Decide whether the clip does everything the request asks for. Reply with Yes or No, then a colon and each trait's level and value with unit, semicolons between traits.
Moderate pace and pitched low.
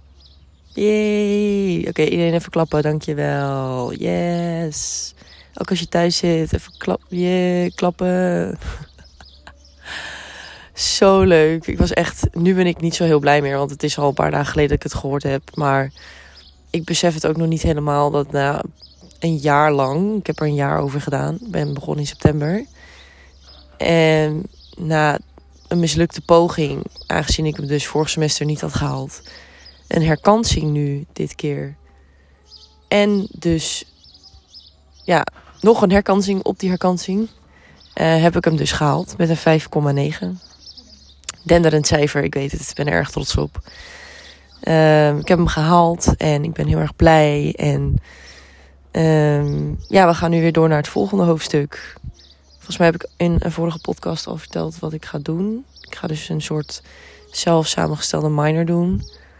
No: average, 165 wpm; medium, 150 Hz